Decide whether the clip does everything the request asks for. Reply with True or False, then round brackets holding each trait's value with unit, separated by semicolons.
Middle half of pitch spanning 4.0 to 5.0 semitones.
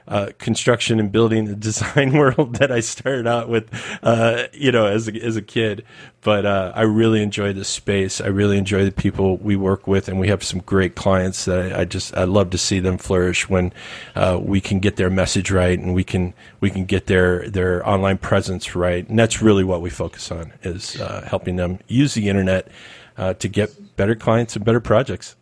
False (3.2 semitones)